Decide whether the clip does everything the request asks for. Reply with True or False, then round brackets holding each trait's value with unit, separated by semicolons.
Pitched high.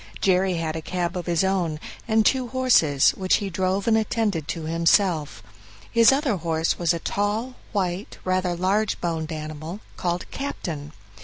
False (180 Hz)